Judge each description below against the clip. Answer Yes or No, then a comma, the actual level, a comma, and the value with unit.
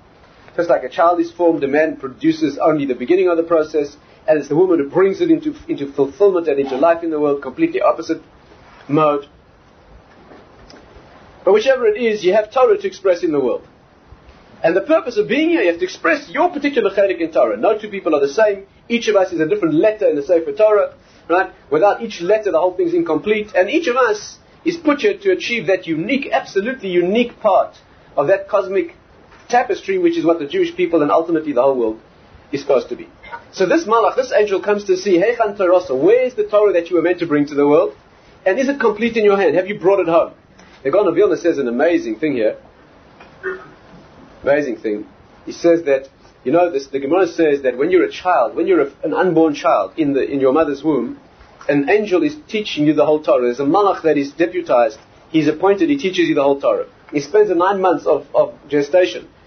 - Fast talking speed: Yes, fast, 220 wpm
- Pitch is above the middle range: Yes, high, 195 Hz